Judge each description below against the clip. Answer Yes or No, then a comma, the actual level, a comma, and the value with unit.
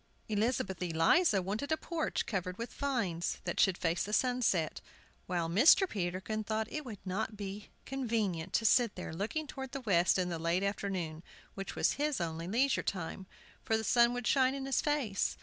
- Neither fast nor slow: Yes, average, 185 wpm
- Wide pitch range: Yes, wide, 5.7 semitones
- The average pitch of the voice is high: Yes, high, 205 Hz